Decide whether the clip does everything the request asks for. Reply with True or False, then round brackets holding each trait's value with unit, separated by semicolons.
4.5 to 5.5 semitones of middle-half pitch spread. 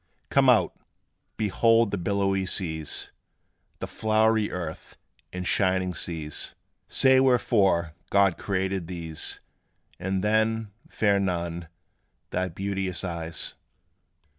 False (3.3 semitones)